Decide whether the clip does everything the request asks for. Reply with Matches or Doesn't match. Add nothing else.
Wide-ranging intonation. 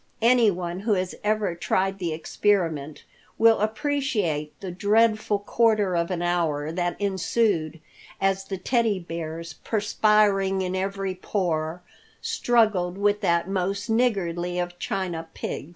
Doesn't match